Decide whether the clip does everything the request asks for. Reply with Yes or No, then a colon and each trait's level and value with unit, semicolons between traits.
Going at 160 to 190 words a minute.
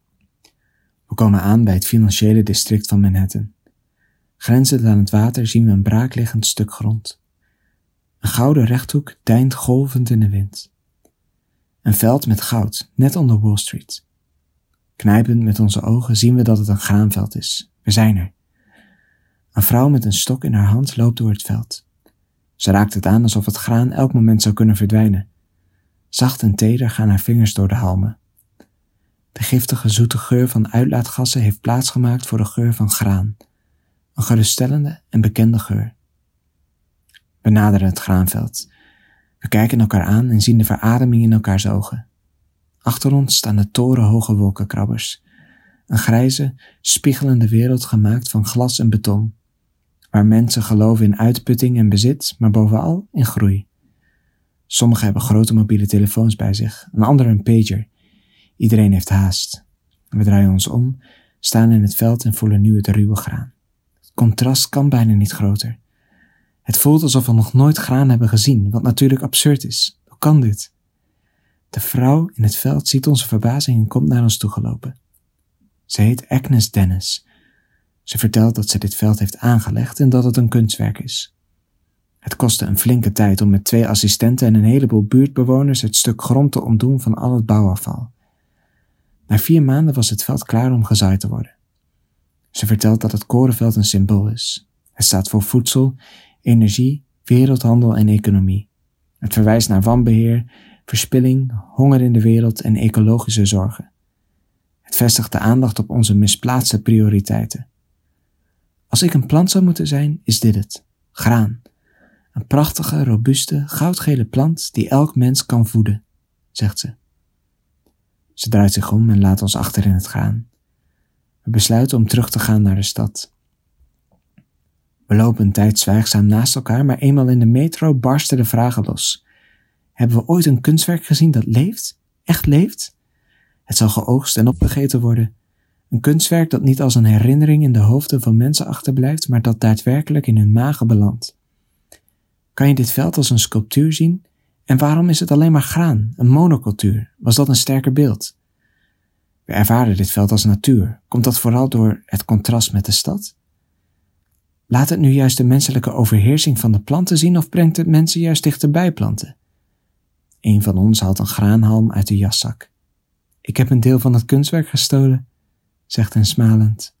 Yes: average, 165 wpm